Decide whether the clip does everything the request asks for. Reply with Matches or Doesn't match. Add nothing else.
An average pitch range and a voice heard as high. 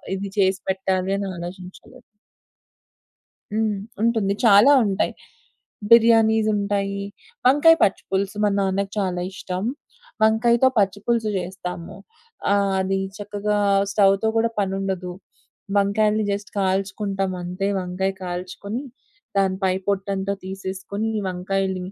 Doesn't match